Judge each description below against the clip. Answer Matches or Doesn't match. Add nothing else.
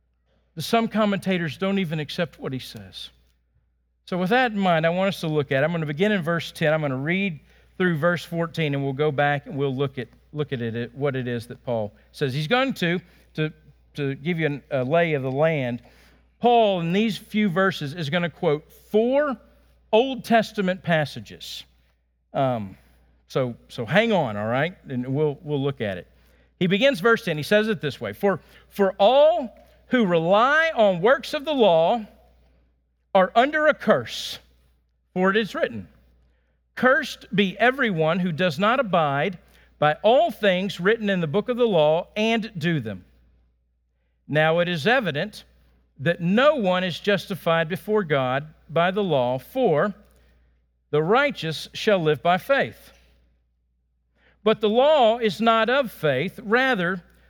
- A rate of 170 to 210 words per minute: Matches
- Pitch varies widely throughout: Matches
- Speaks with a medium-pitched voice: Matches